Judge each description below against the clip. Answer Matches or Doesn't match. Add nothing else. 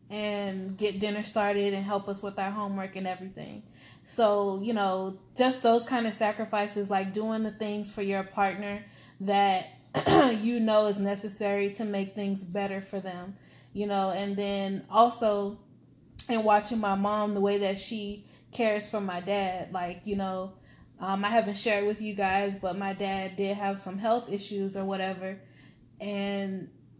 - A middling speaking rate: Matches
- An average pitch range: Doesn't match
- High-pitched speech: Matches